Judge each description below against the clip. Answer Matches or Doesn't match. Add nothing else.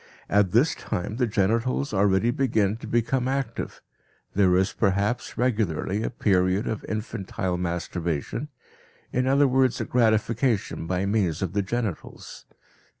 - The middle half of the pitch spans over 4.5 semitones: Doesn't match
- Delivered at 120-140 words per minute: Matches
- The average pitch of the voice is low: Matches